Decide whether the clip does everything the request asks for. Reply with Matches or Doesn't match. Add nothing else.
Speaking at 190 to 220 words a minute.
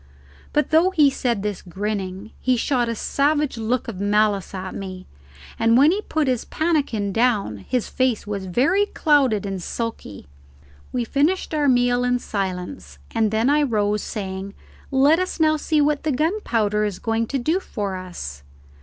Doesn't match